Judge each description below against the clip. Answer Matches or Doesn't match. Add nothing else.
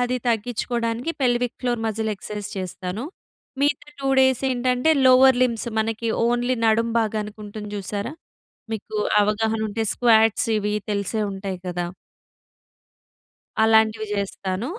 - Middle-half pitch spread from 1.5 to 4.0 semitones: Matches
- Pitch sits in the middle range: Doesn't match